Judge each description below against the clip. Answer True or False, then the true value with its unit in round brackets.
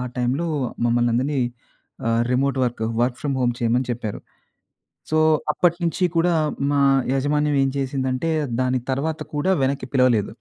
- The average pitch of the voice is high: False (130 Hz)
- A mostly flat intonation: False (3.2 semitones)